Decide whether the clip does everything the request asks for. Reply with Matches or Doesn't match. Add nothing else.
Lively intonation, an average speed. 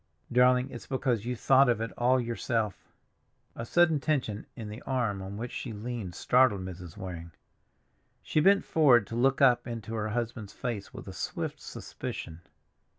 Doesn't match